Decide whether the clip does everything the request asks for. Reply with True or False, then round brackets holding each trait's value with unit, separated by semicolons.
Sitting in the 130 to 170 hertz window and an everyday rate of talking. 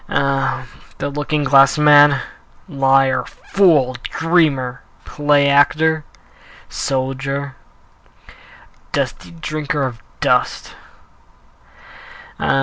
False (140 Hz; 75 wpm)